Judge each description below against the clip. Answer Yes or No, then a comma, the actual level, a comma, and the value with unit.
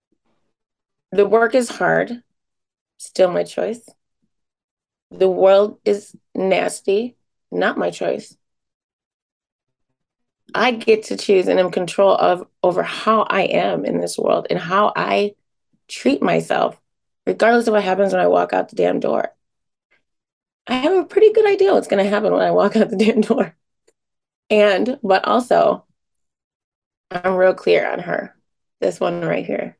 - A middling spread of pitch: Yes, average, 3.5 semitones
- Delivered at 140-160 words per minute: Yes, average, 150 wpm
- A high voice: Yes, high, 205 Hz